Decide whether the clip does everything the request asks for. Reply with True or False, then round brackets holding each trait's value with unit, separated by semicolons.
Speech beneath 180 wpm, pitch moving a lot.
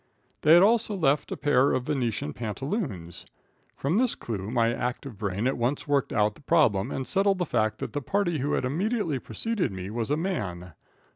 False (195 wpm; 7.8 semitones)